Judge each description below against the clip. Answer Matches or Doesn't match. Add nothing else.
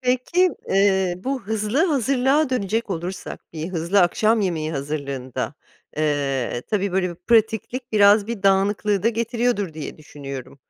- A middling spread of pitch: Doesn't match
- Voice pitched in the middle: Doesn't match